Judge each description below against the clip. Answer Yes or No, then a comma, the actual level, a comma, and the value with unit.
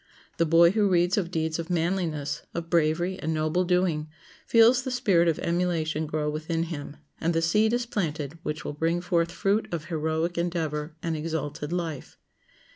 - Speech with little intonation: Yes, narrow, 2.3 semitones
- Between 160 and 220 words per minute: Yes, average, 175 wpm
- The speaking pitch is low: No, medium, 165 Hz